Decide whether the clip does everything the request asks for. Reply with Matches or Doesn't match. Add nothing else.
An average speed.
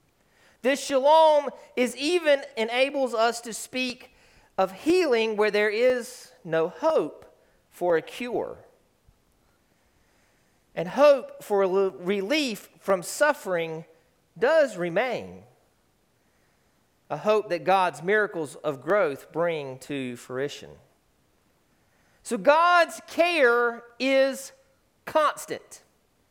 Doesn't match